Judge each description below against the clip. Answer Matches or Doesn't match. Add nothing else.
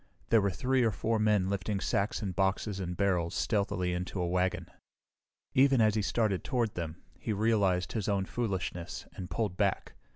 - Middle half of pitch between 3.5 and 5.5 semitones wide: Doesn't match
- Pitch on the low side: Matches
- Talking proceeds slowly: Doesn't match